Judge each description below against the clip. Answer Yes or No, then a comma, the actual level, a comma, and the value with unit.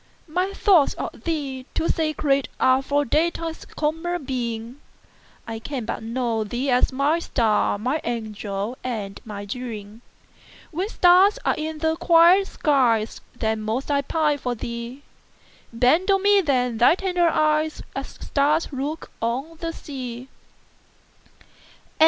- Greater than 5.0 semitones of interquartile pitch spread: Yes, wide, 5.5 semitones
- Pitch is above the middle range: Yes, very high, 275 Hz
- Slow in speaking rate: Yes, slow, 115 wpm